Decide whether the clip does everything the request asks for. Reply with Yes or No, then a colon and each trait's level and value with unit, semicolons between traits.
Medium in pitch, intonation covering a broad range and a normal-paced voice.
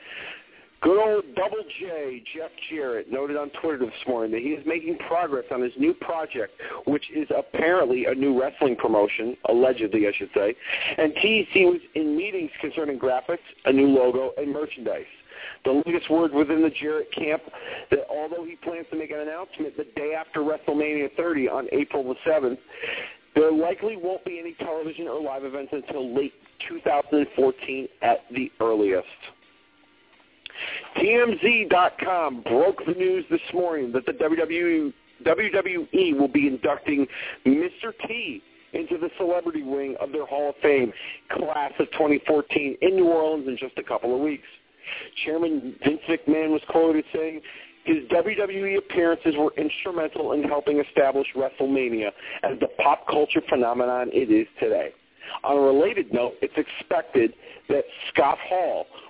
No: medium, 155 Hz; average, 4.9 semitones; average, 150 wpm